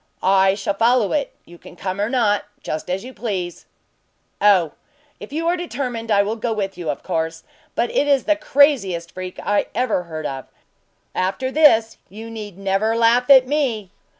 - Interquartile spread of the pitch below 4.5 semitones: No, average, 5.3 semitones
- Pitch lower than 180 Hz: No, high, 215 Hz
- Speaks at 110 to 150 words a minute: No, average, 180 wpm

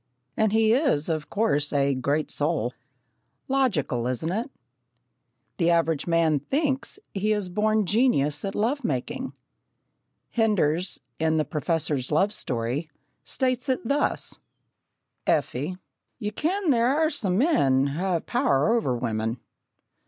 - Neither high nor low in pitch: Yes, medium, 180 Hz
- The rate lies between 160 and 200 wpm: No, slow, 135 wpm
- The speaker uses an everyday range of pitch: No, wide, 8.2 semitones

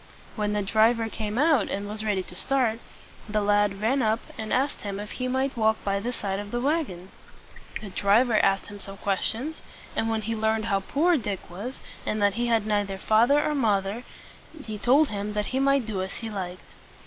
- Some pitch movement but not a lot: Yes, average, 3.1 semitones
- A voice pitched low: No, high, 215 Hz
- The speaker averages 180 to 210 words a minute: Yes, fast, 205 wpm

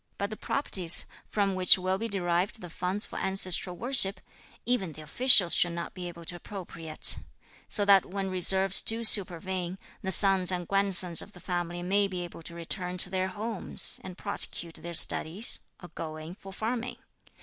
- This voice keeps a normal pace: Yes, average, 180 wpm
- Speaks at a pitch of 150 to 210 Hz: Yes, medium, 185 Hz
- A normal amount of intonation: No, narrow, 2.3 semitones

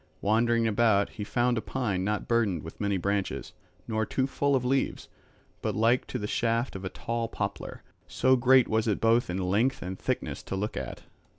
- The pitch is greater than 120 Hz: No, low, 115 Hz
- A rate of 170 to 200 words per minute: Yes, average, 195 wpm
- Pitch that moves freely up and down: No, average, 3.2 semitones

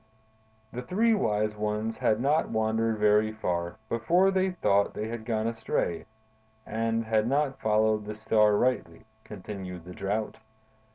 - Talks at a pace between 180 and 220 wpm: No, average, 140 wpm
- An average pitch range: No, narrow, 1.8 semitones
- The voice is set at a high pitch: No, low, 110 Hz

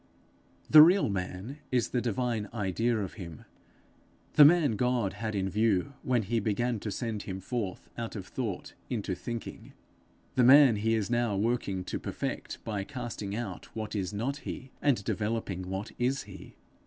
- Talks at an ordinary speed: Yes, average, 165 wpm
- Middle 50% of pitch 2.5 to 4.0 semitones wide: Yes, average, 3.7 semitones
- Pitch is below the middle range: Yes, low, 110 Hz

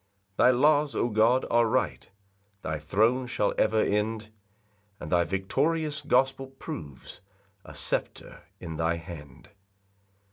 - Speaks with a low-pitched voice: Yes, low, 110 Hz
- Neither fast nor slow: No, slow, 130 wpm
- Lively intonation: Yes, wide, 7.7 semitones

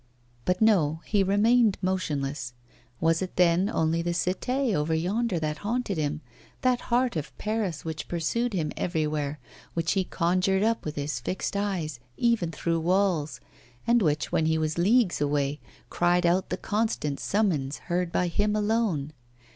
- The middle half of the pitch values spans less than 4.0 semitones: No, average, 4.9 semitones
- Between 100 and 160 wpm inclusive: Yes, average, 155 wpm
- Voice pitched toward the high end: No, medium, 175 Hz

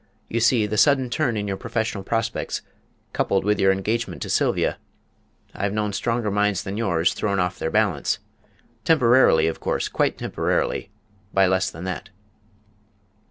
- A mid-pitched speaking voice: No, low, 105 Hz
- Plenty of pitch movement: No, average, 3.2 semitones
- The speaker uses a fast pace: No, average, 155 wpm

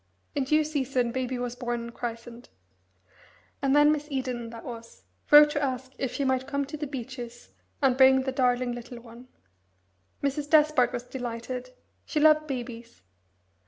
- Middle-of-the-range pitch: No, very high, 255 Hz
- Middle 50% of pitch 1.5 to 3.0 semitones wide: Yes, narrow, 2.6 semitones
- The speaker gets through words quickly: No, average, 160 wpm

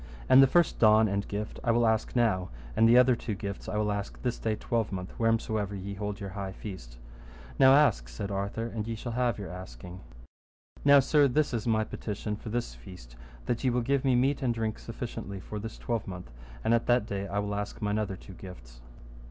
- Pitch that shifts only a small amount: No, average, 3.3 semitones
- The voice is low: Yes, low, 110 Hz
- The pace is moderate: No, fast, 215 wpm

